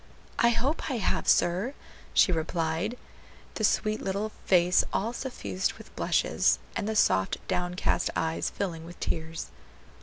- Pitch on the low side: No, medium, 185 Hz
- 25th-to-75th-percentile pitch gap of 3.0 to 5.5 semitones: Yes, average, 4.8 semitones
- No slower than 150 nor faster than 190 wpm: No, average, 140 wpm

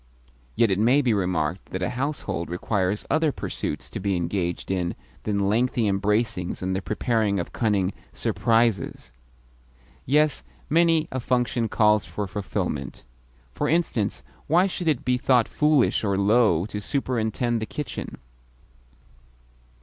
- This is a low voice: Yes, low, 110 Hz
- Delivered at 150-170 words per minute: No, slow, 135 wpm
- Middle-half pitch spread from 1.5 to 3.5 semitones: No, average, 4.7 semitones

